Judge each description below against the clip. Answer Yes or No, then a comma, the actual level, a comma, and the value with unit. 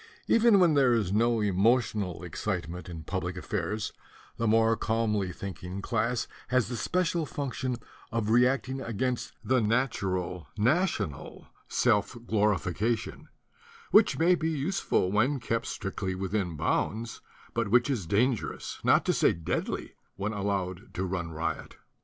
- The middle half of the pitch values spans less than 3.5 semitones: No, average, 4.8 semitones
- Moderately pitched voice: No, low, 110 Hz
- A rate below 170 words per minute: Yes, average, 140 wpm